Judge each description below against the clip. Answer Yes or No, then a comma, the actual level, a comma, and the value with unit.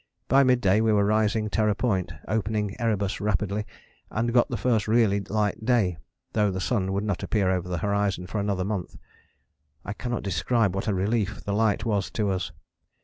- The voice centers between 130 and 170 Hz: No, low, 105 Hz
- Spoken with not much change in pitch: Yes, narrow, 2.2 semitones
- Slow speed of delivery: No, average, 190 wpm